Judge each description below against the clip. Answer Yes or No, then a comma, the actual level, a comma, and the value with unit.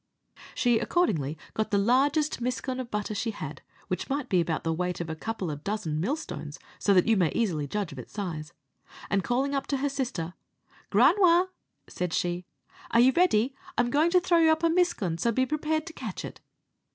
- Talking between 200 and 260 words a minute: Yes, fast, 205 wpm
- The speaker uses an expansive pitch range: Yes, wide, 8.4 semitones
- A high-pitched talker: Yes, high, 225 Hz